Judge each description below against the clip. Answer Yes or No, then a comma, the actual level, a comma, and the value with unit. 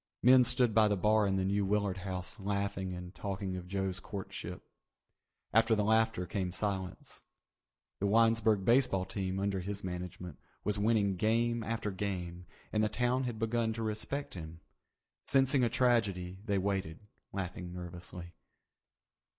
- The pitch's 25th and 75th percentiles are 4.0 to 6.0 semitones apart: No, average, 3.3 semitones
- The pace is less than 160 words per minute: Yes, average, 150 wpm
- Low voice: Yes, low, 100 Hz